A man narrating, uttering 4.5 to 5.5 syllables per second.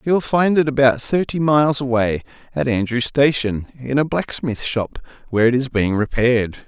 Yes: male; 5.2 syllables/s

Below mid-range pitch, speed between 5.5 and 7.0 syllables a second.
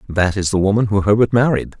Yes: low, 105 Hz; 6.3 syllables/s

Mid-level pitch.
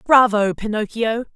No: high, 220 Hz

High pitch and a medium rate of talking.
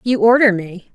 Yes: high, 215 Hz; average, 190 wpm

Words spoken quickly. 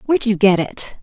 Yes: fast, 235 wpm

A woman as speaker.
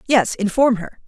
Yes: female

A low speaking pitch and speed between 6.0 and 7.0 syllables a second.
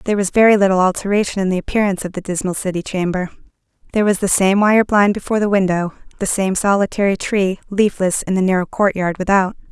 No: high, 195 Hz; 6.5 syllables/s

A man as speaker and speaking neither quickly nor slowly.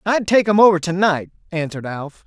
Yes: male; average, 185 wpm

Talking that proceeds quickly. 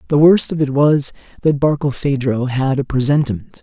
No: average, 165 wpm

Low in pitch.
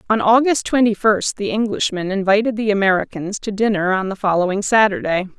No: high, 205 Hz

